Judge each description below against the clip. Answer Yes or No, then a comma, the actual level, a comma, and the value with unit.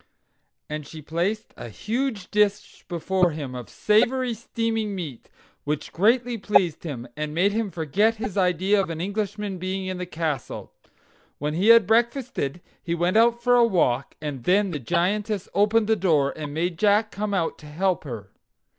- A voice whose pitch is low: No, high, 190 Hz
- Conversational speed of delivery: Yes, average, 170 wpm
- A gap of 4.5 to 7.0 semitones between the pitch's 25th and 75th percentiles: Yes, average, 5.0 semitones